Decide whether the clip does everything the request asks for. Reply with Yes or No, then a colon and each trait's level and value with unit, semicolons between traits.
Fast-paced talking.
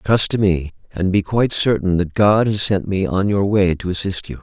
Yes: fast, 245 wpm